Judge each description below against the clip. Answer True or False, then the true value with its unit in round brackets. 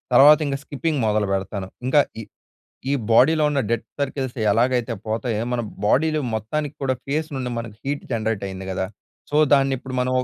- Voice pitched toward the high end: False (130 Hz)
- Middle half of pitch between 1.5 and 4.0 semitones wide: False (4.5 semitones)